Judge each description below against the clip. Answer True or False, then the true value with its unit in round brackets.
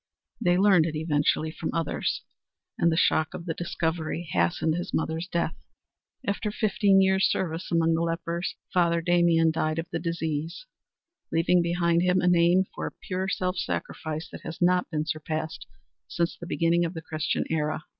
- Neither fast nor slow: True (165 wpm)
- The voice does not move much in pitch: True (1.8 semitones)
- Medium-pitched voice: True (170 Hz)